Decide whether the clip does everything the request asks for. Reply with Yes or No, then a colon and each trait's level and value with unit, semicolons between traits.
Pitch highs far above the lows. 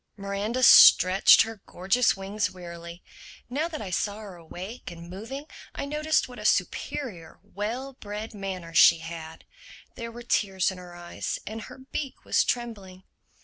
No: average, 4.8 semitones